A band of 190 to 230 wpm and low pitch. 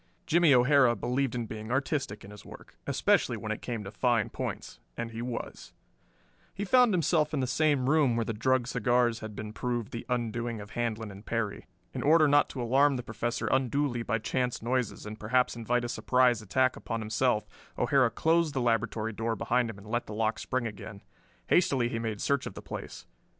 Yes: average, 200 wpm; low, 120 Hz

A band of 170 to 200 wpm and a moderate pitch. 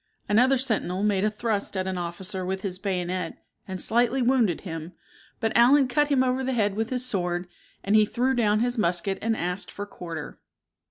No: average, 195 wpm; high, 205 Hz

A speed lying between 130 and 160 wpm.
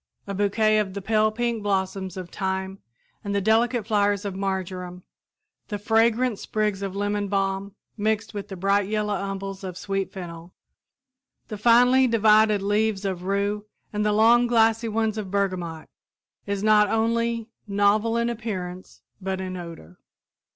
Yes: average, 150 wpm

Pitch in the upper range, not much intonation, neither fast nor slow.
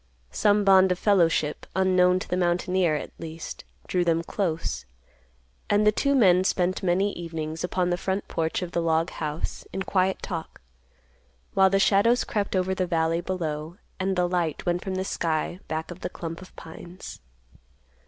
No: medium, 180 Hz; narrow, 2.3 semitones; average, 175 wpm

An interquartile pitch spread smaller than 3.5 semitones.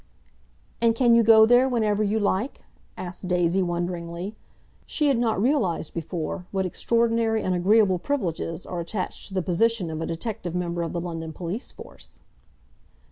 No: average, 4.7 semitones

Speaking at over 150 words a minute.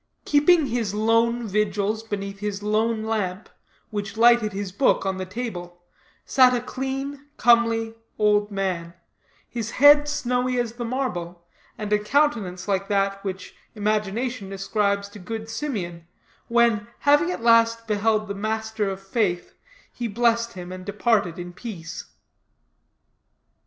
No: slow, 135 wpm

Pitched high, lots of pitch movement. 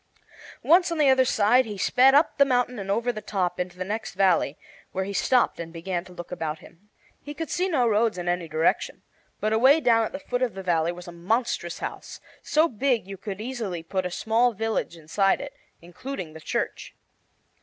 Yes: high, 210 Hz; wide, 5.9 semitones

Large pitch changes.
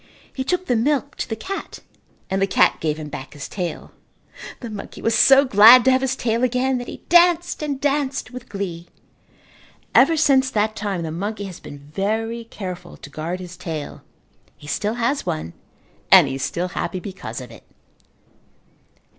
Yes: wide, 7.1 semitones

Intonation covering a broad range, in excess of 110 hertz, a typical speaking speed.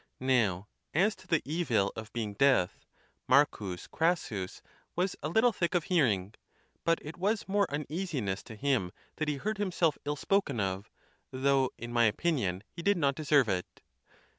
Yes: wide, 7.8 semitones; medium, 140 Hz; average, 165 wpm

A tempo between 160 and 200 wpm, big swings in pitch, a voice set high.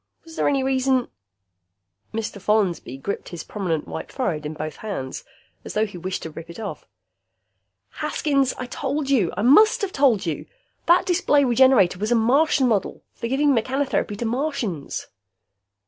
Yes: average, 165 wpm; wide, 7.2 semitones; high, 225 Hz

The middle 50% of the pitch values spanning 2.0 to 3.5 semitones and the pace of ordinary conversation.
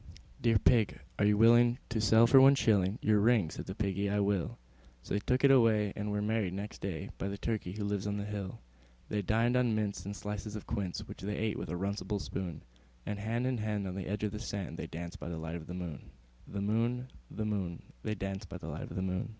No: narrow, 2.4 semitones; fast, 245 wpm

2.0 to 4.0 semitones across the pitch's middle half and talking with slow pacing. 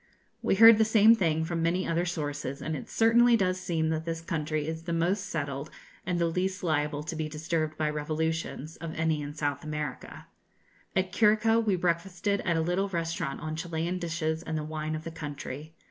No: average, 2.8 semitones; average, 195 wpm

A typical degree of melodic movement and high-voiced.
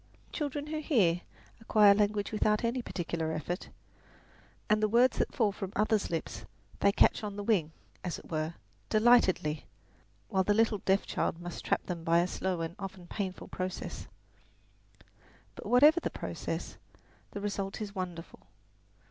Yes: average, 3.7 semitones; high, 200 Hz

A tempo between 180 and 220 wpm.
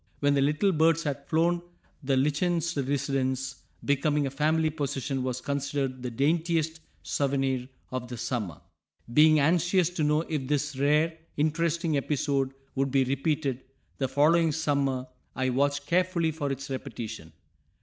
No: average, 140 wpm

